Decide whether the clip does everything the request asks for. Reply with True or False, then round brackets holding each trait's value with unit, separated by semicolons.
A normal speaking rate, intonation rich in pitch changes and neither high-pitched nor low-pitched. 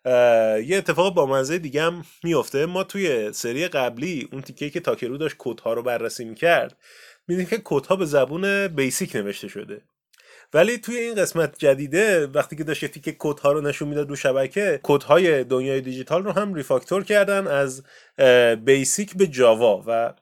False (165 wpm; 6.1 semitones; 150 Hz)